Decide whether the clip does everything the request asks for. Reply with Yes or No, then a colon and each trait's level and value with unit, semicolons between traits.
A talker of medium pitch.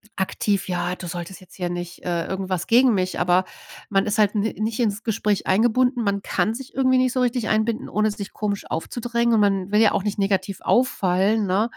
No: high, 205 Hz